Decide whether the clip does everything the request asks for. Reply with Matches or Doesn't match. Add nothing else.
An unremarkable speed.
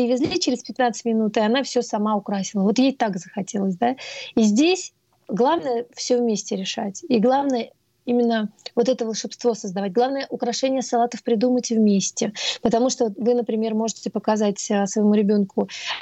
Matches